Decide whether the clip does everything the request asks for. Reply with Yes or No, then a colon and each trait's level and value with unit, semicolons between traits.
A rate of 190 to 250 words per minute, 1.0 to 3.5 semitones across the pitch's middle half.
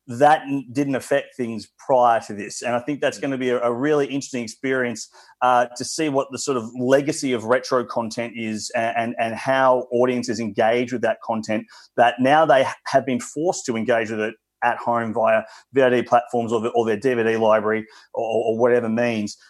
Yes: average, 200 wpm; narrow, 2.4 semitones